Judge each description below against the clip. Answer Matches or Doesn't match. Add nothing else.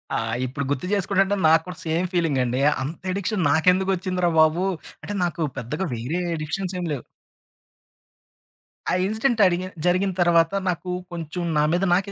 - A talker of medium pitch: Matches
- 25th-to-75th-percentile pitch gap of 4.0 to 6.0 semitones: Doesn't match